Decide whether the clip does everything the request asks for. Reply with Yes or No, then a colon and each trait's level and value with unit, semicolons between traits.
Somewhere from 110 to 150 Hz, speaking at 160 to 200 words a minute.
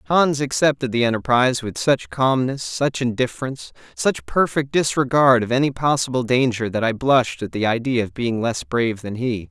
Yes: low, 125 Hz; average, 175 wpm